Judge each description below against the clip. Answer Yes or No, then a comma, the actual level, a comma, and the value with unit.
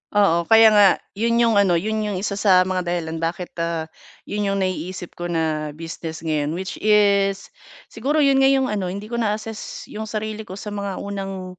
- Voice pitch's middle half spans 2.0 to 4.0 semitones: Yes, average, 3.5 semitones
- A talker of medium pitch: No, high, 195 Hz